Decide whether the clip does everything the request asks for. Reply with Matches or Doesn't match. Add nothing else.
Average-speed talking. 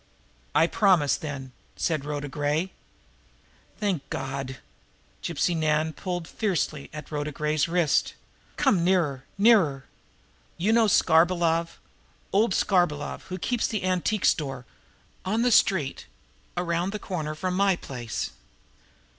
Doesn't match